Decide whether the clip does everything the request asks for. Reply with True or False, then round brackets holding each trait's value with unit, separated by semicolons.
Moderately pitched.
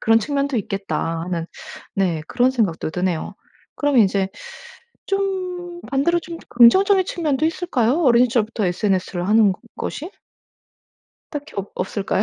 False (235 Hz)